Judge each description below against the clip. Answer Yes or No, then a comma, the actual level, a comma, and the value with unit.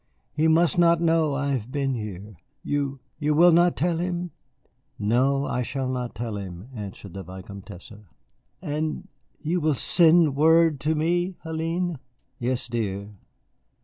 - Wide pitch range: Yes, wide, 6.5 semitones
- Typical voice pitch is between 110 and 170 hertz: Yes, medium, 140 Hz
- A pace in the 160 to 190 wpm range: No, average, 145 wpm